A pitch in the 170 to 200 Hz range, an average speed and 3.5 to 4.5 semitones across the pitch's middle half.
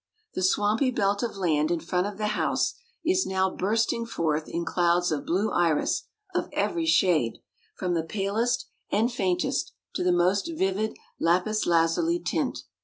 Yes: high, 190 Hz; average, 160 wpm; average, 4.1 semitones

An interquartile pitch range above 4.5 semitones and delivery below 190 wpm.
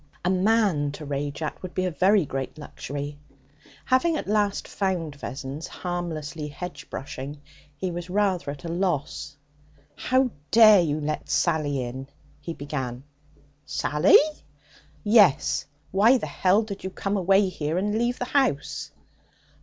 Yes: wide, 5.5 semitones; average, 145 wpm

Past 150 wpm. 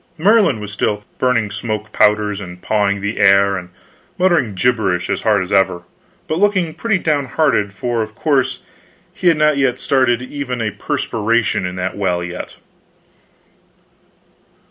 No: average, 145 wpm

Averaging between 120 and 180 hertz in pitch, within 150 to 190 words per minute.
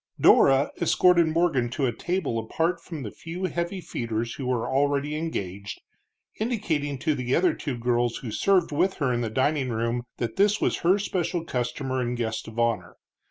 Yes: medium, 140 Hz; average, 180 wpm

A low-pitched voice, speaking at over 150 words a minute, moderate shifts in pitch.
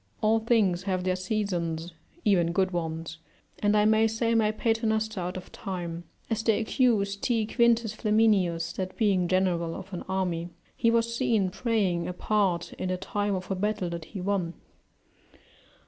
No: high, 195 Hz; average, 165 wpm; average, 3.6 semitones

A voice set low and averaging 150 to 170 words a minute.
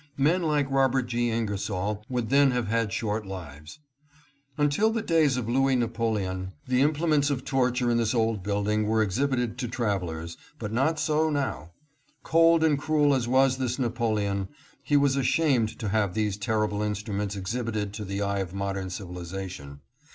Yes: low, 115 Hz; average, 165 wpm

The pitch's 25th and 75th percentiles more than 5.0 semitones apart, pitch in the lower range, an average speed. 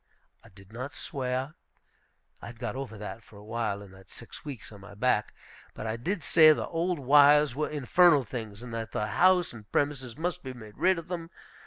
No: wide, 5.5 semitones; low, 125 Hz; fast, 210 wpm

